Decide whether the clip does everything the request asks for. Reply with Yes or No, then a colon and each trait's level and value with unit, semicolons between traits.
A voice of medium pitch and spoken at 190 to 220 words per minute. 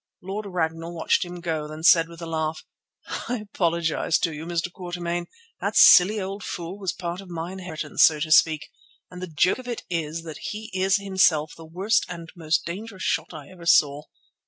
Yes: medium, 170 Hz; average, 195 wpm